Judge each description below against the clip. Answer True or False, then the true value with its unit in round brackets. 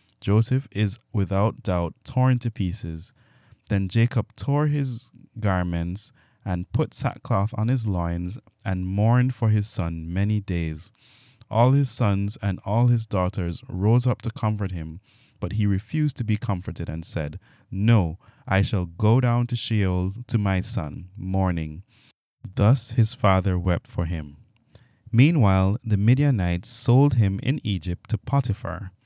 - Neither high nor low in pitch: False (105 Hz)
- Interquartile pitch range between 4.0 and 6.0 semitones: True (4.4 semitones)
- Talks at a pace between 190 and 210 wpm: False (145 wpm)